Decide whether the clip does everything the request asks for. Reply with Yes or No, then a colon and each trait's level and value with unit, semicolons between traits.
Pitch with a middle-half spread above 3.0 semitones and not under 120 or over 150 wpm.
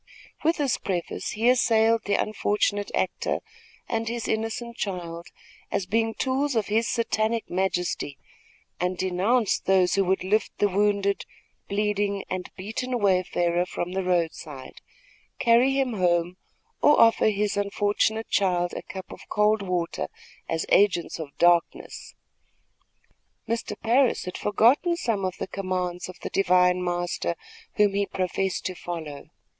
Yes: average, 3.7 semitones; average, 140 wpm